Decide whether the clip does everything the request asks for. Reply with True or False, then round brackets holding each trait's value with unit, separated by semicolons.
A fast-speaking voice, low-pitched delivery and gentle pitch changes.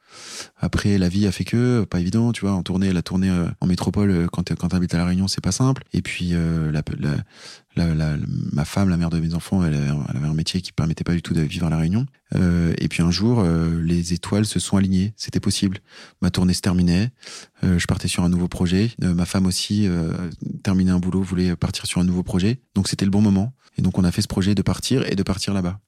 True (260 wpm; 90 Hz; 2.2 semitones)